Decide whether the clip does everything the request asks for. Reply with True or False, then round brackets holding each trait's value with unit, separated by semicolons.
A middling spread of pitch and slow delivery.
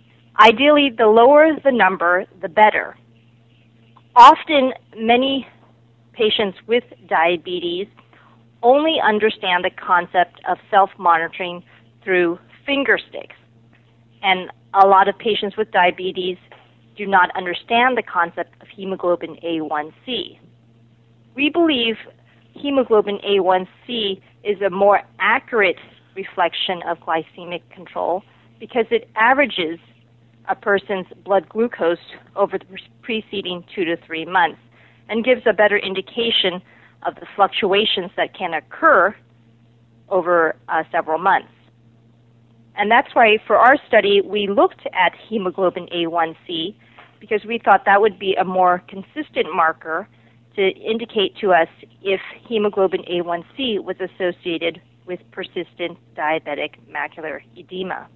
True (5.0 semitones; 115 wpm)